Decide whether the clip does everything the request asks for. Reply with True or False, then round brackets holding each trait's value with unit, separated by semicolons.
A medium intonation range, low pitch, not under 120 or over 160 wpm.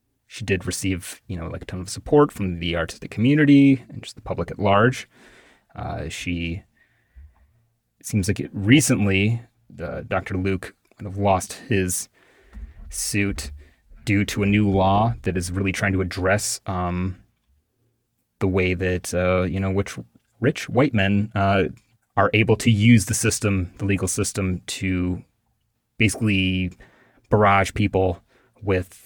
True (3.5 semitones; 100 Hz; 150 wpm)